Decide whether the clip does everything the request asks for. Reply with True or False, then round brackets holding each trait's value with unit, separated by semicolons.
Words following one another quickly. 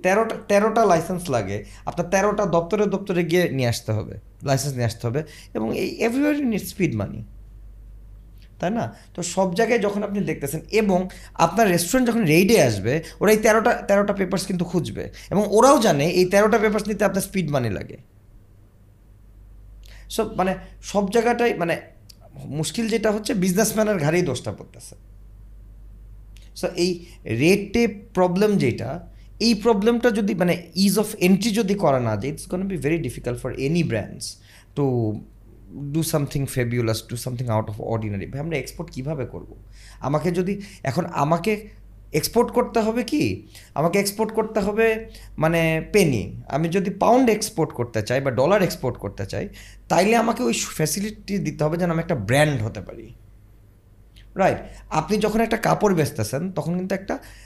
True (155 wpm)